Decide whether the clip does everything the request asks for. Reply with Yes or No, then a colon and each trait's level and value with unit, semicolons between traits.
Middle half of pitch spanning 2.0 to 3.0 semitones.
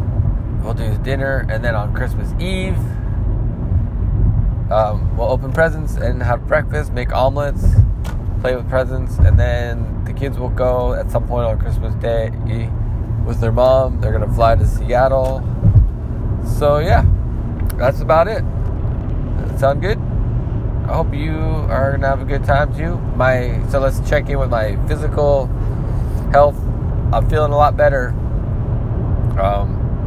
Yes: narrow, 2.6 semitones